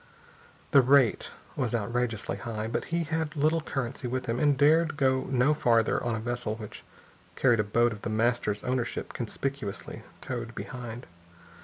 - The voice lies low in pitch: Yes, low, 120 Hz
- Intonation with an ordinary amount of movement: Yes, average, 3.2 semitones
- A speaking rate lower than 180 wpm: Yes, average, 160 wpm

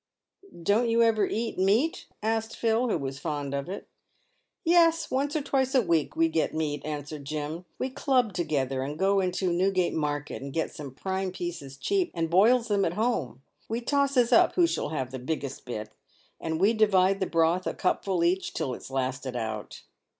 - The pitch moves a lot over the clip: Yes, wide, 7.5 semitones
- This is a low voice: No, medium, 180 Hz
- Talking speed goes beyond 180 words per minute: Yes, average, 200 wpm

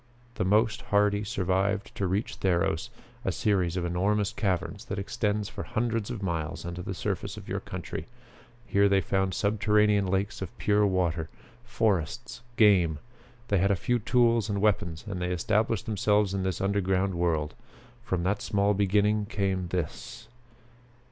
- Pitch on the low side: Yes, low, 100 Hz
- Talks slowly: No, average, 155 wpm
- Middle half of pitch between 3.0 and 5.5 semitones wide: No, narrow, 2.4 semitones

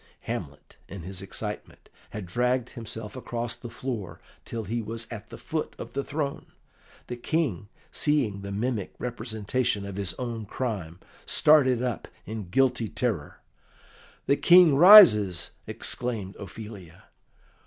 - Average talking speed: No, slow, 130 wpm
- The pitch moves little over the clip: No, average, 4.2 semitones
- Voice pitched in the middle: No, low, 115 Hz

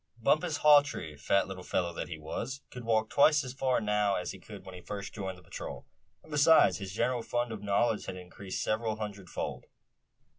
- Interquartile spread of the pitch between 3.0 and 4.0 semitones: No, average, 5.3 semitones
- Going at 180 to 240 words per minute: Yes, average, 190 wpm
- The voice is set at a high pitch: No, low, 105 Hz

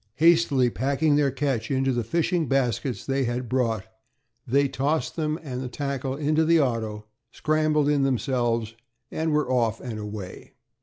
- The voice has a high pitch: No, low, 135 Hz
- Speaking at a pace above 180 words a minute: No, average, 155 wpm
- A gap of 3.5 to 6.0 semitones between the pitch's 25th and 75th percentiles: Yes, average, 3.9 semitones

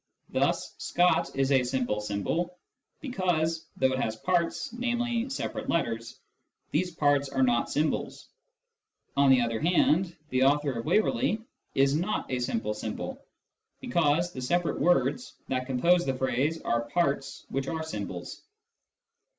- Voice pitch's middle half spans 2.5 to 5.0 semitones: No, wide, 5.4 semitones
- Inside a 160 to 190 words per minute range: No, average, 150 wpm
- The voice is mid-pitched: Yes, medium, 145 Hz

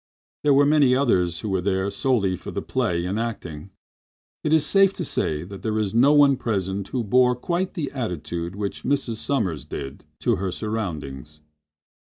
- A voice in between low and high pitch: No, low, 105 Hz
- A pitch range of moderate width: No, wide, 7.1 semitones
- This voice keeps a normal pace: Yes, average, 175 wpm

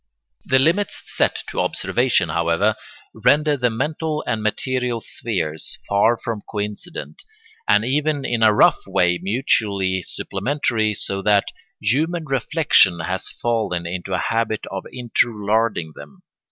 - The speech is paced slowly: Yes, slow, 130 wpm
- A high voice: No, low, 110 Hz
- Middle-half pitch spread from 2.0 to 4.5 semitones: No, average, 5.1 semitones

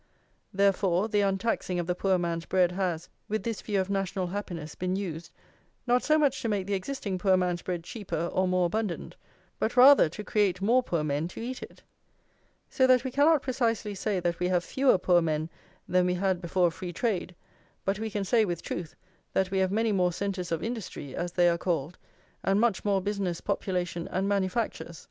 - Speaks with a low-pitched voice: No, high, 190 Hz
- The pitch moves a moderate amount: Yes, average, 3.1 semitones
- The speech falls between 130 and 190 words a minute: No, average, 200 wpm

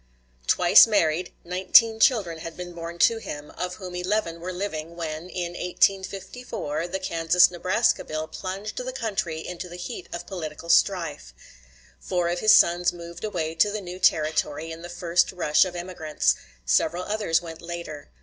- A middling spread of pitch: No, narrow, 2.3 semitones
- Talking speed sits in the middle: Yes, average, 165 wpm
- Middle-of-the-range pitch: Yes, medium, 175 Hz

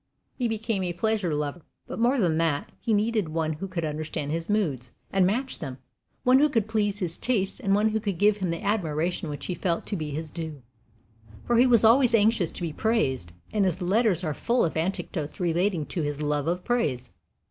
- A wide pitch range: Yes, wide, 5.7 semitones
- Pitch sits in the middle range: Yes, medium, 180 Hz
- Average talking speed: No, fast, 215 wpm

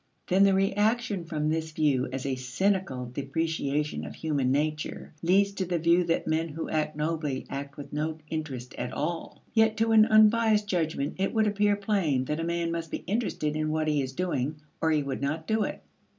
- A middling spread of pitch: Yes, average, 5.0 semitones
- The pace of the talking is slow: No, average, 200 wpm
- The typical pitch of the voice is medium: Yes, medium, 160 Hz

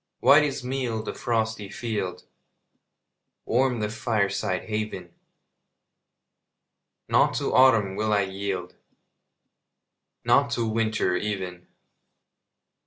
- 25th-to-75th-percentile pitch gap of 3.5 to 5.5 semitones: No, average, 2.9 semitones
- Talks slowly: Yes, slow, 95 wpm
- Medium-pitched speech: No, low, 110 Hz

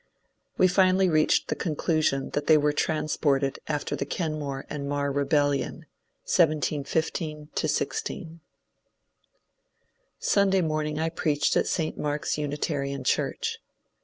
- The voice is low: No, medium, 150 Hz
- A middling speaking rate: No, slow, 110 wpm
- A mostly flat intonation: Yes, narrow, 2.0 semitones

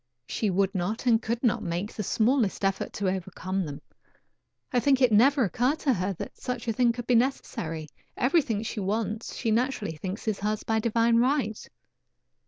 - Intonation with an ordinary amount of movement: Yes, average, 4.0 semitones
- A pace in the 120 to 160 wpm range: No, average, 185 wpm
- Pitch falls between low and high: No, high, 220 Hz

